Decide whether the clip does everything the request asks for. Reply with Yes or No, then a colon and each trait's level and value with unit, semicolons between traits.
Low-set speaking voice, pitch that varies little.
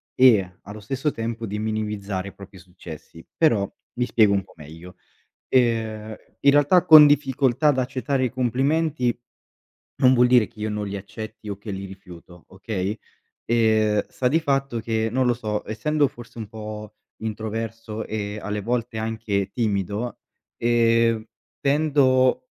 No: low, 110 Hz; average, 3.6 semitones